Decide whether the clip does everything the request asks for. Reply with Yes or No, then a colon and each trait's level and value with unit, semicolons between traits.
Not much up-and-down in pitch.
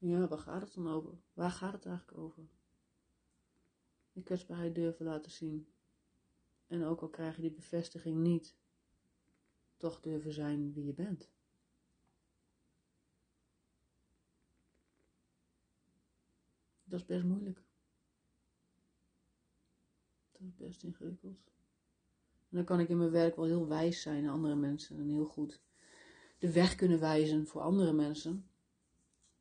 No: average, 3.3 semitones